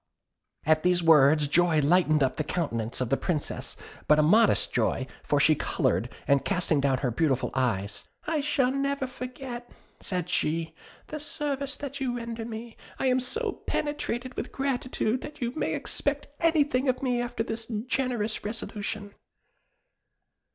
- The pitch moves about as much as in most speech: No, wide, 8.8 semitones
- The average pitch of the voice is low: No, high, 225 Hz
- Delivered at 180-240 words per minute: No, average, 155 wpm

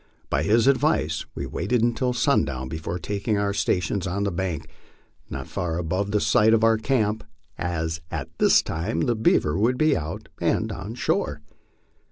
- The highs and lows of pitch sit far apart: Yes, wide, 5.7 semitones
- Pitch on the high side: No, low, 100 Hz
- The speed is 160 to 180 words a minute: Yes, average, 170 wpm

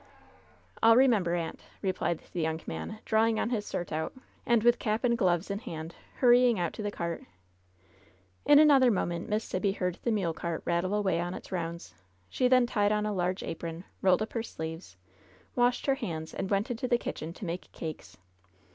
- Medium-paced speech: Yes, average, 190 wpm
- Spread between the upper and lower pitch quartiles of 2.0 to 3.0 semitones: No, average, 5.2 semitones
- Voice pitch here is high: Yes, high, 195 Hz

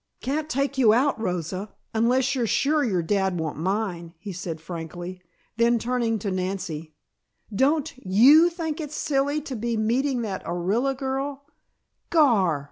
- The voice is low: No, high, 225 Hz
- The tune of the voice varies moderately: No, wide, 6.7 semitones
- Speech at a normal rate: Yes, average, 150 wpm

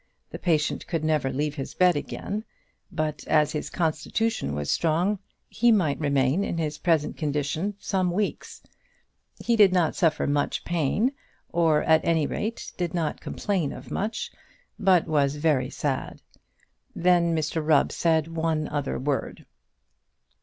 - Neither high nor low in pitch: Yes, medium, 160 Hz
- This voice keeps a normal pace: Yes, average, 145 wpm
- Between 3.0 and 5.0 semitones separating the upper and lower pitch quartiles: Yes, average, 3.4 semitones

